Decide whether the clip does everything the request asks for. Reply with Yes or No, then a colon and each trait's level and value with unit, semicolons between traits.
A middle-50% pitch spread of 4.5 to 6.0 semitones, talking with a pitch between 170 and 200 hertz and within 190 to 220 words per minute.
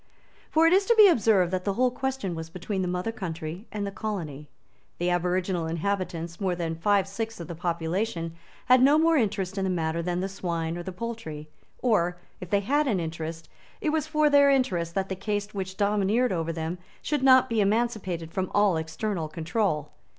Yes: average, 5.0 semitones; high, 190 Hz; average, 200 wpm